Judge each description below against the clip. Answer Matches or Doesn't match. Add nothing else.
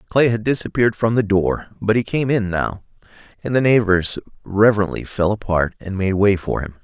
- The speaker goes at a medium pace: Matches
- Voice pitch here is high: Doesn't match